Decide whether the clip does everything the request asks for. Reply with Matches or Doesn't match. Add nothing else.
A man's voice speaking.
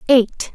Doesn't match